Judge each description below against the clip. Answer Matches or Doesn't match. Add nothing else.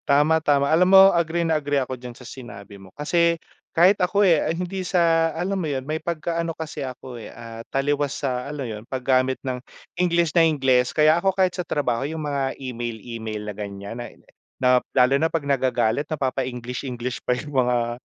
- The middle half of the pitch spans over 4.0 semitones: Matches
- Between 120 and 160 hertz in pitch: Matches